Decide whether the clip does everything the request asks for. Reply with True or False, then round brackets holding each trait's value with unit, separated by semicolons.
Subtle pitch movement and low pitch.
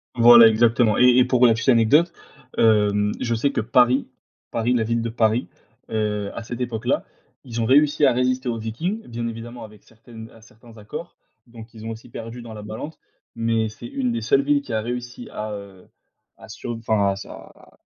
True (1.9 semitones; 115 Hz)